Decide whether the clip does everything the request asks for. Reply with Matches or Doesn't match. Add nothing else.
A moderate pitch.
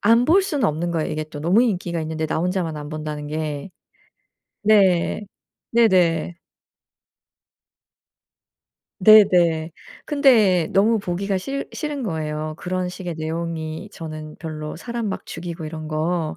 Matches